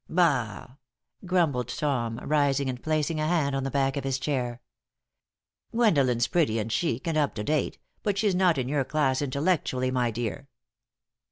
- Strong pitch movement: No, average, 3.7 semitones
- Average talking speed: Yes, average, 165 wpm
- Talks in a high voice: No, medium, 140 Hz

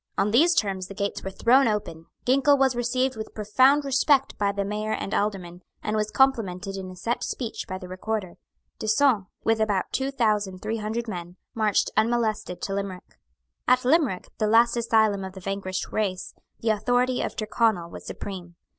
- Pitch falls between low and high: No, high, 215 Hz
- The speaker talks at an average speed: Yes, average, 180 wpm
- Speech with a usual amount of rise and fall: Yes, average, 3.8 semitones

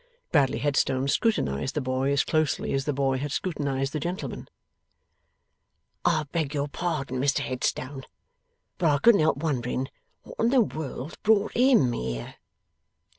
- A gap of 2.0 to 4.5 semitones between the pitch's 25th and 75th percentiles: Yes, average, 3.6 semitones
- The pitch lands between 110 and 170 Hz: Yes, medium, 140 Hz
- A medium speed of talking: Yes, average, 145 wpm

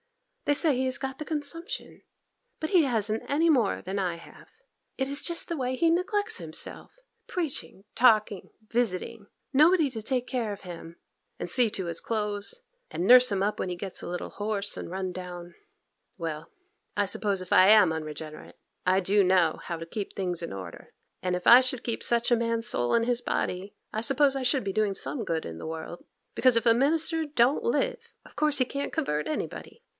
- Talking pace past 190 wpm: Yes, average, 200 wpm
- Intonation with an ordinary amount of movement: No, wide, 7.1 semitones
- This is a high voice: Yes, high, 225 Hz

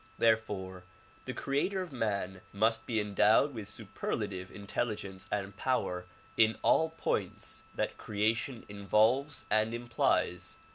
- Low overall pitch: Yes, low, 110 Hz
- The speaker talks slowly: Yes, slow, 125 wpm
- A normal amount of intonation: Yes, average, 3.2 semitones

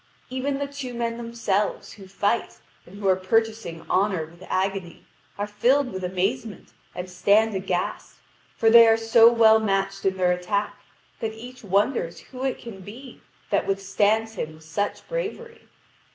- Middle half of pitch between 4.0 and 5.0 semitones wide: No, average, 3.6 semitones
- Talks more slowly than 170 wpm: Yes, average, 160 wpm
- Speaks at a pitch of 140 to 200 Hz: No, high, 210 Hz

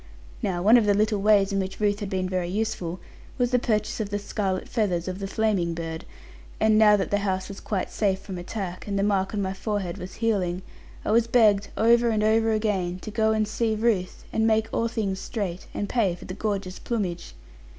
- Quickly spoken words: Yes, fast, 220 wpm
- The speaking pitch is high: Yes, high, 205 Hz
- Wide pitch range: No, average, 2.7 semitones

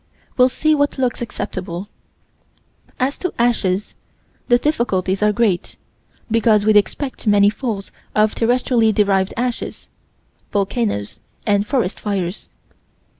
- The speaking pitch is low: No, high, 215 Hz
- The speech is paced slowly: Yes, slow, 115 wpm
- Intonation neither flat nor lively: Yes, average, 3.5 semitones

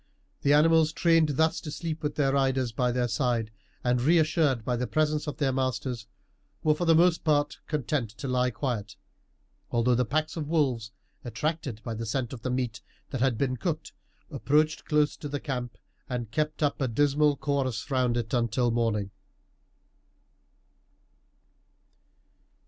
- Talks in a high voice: No, low, 135 Hz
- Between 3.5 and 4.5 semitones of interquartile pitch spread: Yes, average, 3.8 semitones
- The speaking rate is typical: Yes, average, 160 wpm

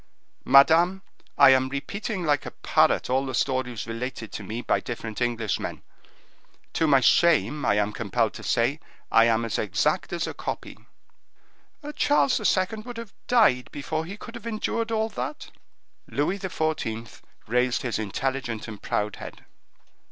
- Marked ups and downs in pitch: Yes, wide, 7.6 semitones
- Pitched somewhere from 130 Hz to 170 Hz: Yes, low, 135 Hz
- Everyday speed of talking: Yes, average, 150 wpm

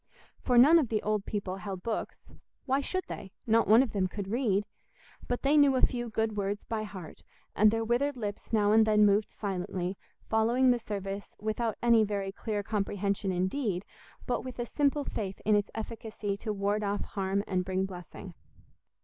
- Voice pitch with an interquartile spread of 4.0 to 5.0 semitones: No, average, 3.0 semitones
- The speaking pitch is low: No, high, 210 Hz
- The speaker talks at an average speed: Yes, average, 185 wpm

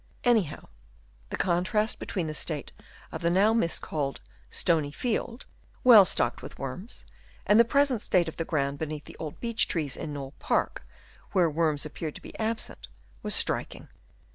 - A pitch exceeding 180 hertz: No, medium, 170 Hz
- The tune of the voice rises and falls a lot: Yes, wide, 6.4 semitones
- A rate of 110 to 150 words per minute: No, average, 170 wpm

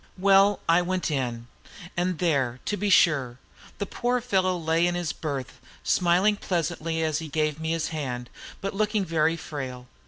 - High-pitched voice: No, medium, 165 Hz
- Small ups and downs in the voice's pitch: No, average, 3.8 semitones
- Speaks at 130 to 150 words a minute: No, average, 165 wpm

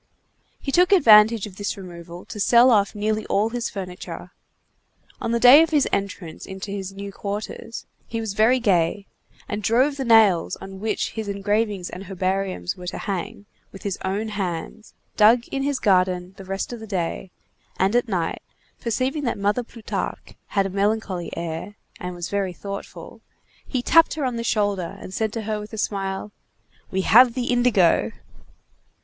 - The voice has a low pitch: No, high, 205 Hz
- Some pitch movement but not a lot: Yes, average, 3.2 semitones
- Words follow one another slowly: No, average, 175 wpm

